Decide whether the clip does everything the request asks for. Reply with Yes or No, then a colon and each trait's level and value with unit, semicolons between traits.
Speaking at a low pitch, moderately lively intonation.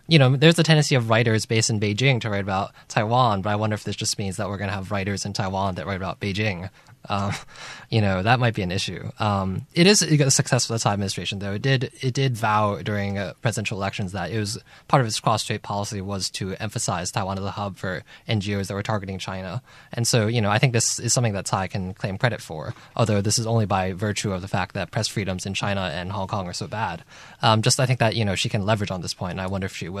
Yes: low, 105 Hz; average, 3.2 semitones